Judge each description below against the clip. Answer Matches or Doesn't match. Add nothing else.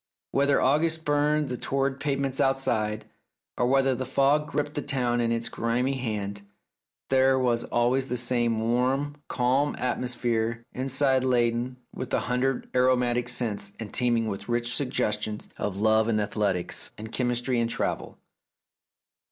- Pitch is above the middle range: Doesn't match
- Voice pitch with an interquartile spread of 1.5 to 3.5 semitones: Matches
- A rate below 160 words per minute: Matches